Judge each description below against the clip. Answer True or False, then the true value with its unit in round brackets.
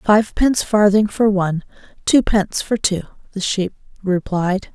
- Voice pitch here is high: True (200 Hz)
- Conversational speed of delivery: False (115 wpm)